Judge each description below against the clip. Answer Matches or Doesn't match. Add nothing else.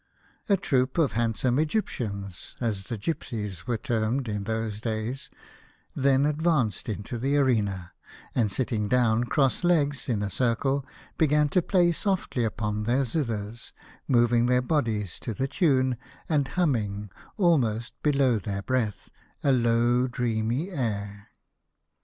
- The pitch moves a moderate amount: Matches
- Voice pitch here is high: Doesn't match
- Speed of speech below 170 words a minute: Matches